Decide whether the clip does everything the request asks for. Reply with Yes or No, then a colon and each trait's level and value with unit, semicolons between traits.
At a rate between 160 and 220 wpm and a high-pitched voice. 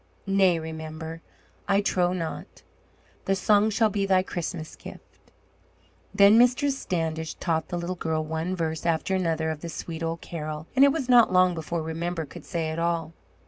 No: average, 175 wpm; medium, 170 Hz